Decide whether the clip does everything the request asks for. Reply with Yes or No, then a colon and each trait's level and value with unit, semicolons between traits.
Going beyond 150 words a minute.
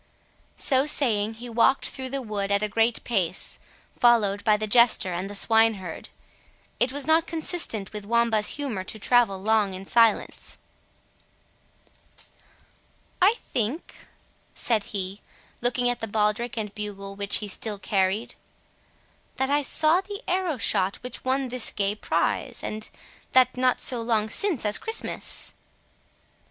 No: average, 145 wpm